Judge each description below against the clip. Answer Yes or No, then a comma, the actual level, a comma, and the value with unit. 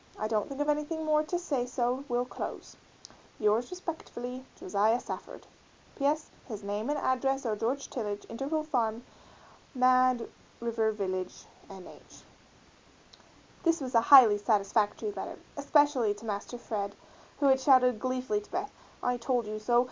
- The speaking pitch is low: No, high, 245 Hz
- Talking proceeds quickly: No, average, 155 wpm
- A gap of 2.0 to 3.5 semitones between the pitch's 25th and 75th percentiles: No, average, 4.5 semitones